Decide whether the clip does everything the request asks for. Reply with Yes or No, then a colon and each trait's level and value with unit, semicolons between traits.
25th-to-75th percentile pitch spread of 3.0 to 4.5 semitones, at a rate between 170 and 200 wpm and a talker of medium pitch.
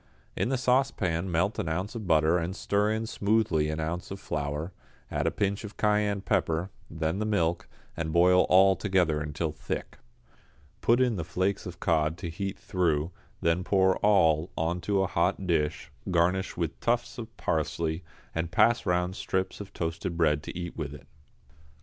No: average, 3.6 semitones; average, 175 wpm; very low, 90 Hz